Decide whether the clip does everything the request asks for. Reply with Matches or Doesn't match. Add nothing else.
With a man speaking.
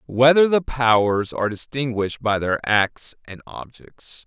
Matches